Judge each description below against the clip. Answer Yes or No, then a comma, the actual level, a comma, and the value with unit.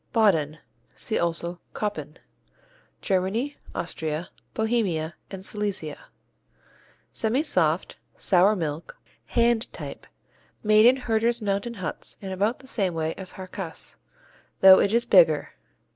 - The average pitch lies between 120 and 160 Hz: No, high, 200 Hz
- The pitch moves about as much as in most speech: Yes, average, 4.9 semitones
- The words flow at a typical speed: No, slow, 115 wpm